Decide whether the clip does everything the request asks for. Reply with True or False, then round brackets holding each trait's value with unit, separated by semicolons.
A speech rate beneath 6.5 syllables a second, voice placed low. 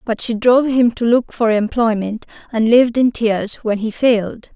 False (4.8 syllables/s; 230 Hz)